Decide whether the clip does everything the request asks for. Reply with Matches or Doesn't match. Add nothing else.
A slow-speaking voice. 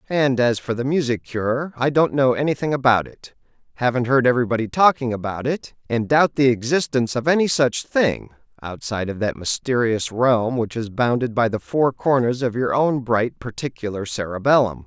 Doesn't match